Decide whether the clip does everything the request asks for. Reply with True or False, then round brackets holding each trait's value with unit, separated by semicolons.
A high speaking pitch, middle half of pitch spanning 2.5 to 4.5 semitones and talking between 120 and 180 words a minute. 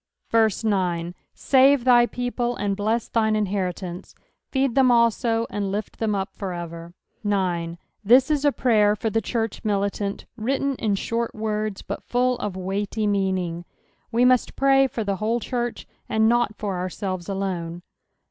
True (215 Hz; 3.8 semitones; 155 wpm)